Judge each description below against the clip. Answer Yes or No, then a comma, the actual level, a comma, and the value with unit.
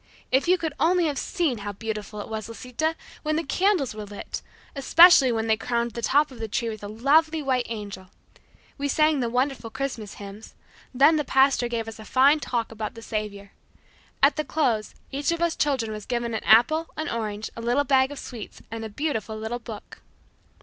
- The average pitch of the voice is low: No, high, 240 Hz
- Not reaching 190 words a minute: No, fast, 205 wpm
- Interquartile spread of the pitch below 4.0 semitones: No, average, 4.8 semitones